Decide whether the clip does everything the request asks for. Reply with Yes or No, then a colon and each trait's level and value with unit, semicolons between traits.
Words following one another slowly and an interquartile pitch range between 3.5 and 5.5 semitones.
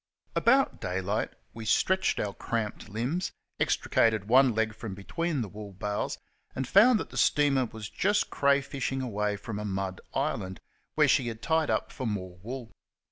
No: average, 165 wpm; average, 4.9 semitones